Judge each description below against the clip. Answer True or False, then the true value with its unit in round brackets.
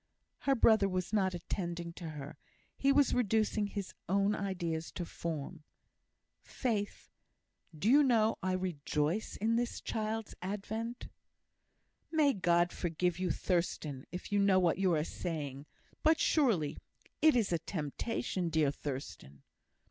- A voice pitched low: False (185 Hz)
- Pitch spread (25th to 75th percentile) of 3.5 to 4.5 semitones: False (4.9 semitones)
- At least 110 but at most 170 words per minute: True (135 wpm)